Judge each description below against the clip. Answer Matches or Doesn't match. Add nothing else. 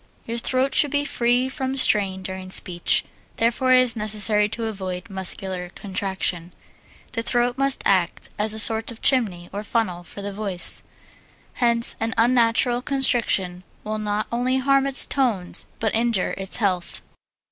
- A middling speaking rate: Matches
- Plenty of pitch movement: Doesn't match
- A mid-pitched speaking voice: Doesn't match